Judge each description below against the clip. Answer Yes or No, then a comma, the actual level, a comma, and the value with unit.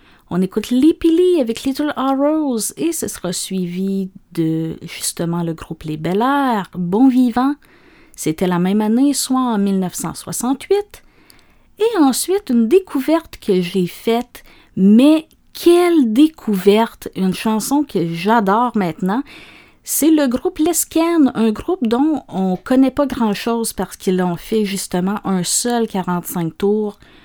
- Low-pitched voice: No, high, 230 Hz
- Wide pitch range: Yes, wide, 7.3 semitones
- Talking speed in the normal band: No, slow, 140 wpm